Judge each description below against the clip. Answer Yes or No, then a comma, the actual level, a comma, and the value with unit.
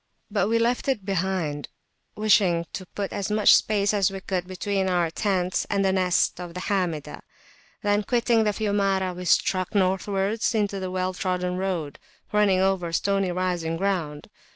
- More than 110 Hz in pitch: Yes, high, 190 Hz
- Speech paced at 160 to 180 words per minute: Yes, average, 165 wpm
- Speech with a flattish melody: Yes, narrow, 2.0 semitones